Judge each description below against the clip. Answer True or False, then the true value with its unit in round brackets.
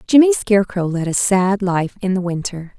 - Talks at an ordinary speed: True (195 wpm)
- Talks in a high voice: True (195 Hz)